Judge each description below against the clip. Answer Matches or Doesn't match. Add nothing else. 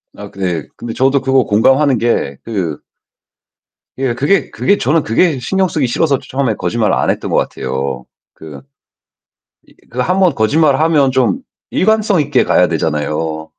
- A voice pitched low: Matches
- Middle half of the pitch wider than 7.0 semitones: Matches